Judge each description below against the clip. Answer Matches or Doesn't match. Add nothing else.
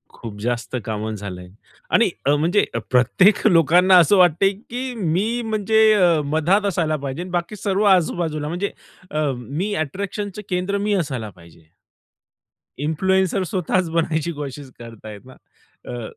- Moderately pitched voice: Matches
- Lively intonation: Matches